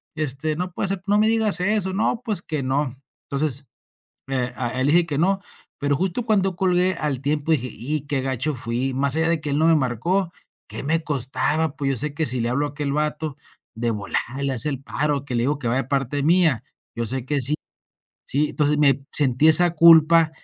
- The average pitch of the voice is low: No, medium, 150 Hz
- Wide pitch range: No, average, 3.7 semitones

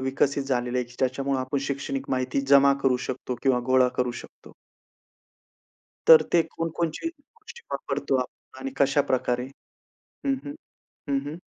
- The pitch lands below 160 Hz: Yes, low, 135 Hz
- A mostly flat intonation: Yes, narrow, 2.1 semitones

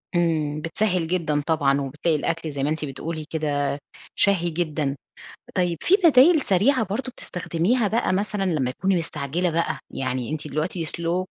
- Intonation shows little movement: No, average, 3.7 semitones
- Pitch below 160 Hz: No, medium, 165 Hz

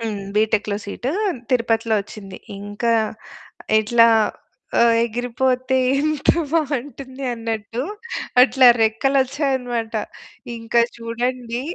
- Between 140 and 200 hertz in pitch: No, high, 235 Hz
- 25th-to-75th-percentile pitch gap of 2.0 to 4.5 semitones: Yes, average, 2.7 semitones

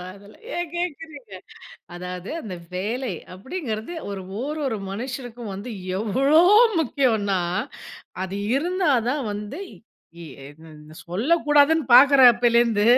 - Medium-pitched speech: No, high, 240 Hz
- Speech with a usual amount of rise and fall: No, wide, 6.3 semitones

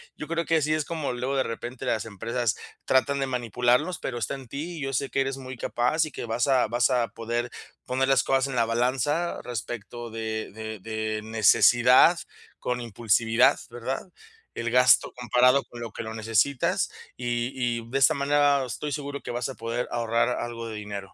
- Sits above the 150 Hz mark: No, low, 120 Hz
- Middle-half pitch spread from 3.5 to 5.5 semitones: No, average, 2.8 semitones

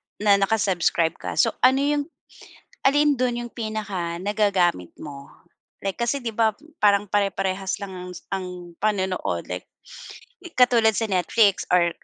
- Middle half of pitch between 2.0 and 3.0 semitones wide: No, average, 3.5 semitones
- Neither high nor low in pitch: No, high, 205 Hz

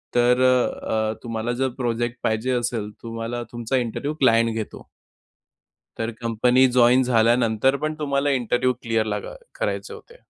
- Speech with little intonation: Yes, narrow, 2.0 semitones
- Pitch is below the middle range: Yes, low, 120 Hz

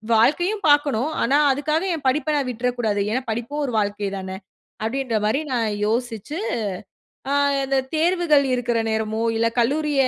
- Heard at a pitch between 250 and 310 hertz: Yes, very high, 255 Hz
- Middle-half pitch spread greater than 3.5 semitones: Yes, average, 4.7 semitones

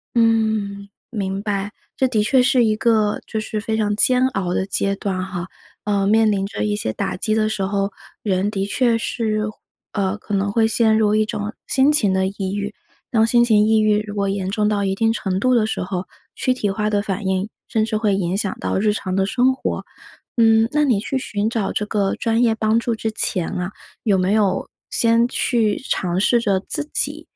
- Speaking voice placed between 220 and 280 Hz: No, high, 210 Hz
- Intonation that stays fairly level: Yes, narrow, 2.2 semitones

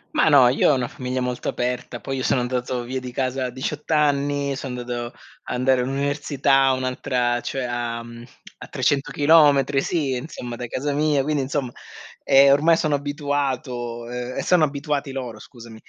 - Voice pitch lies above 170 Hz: No, low, 130 Hz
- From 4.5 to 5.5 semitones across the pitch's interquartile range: No, narrow, 2.5 semitones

